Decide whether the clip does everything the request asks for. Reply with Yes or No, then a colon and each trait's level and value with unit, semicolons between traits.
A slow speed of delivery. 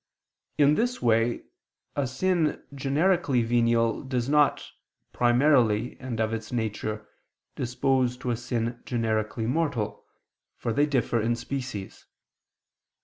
Yes: slow, 115 wpm